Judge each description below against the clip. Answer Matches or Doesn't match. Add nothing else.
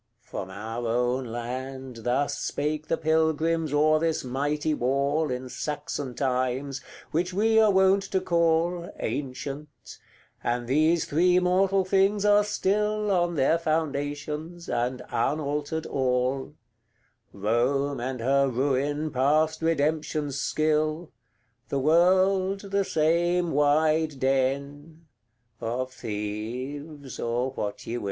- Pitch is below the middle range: Doesn't match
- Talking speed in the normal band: Doesn't match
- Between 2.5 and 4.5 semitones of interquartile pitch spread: Matches